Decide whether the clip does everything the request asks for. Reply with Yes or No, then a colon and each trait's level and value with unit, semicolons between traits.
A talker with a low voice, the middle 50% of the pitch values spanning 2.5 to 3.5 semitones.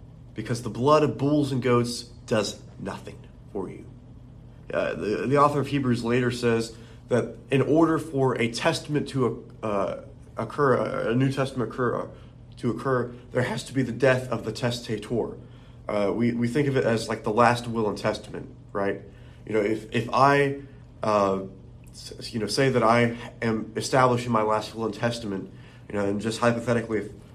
Yes: low, 120 Hz; average, 2.8 semitones